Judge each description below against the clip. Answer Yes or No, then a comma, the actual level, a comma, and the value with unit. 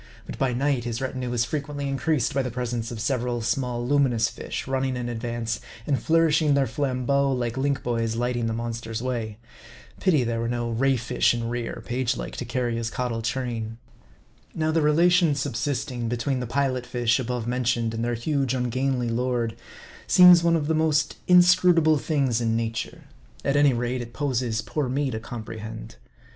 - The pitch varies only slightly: No, average, 3.2 semitones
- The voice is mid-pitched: No, low, 125 Hz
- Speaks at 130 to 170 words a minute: No, average, 180 wpm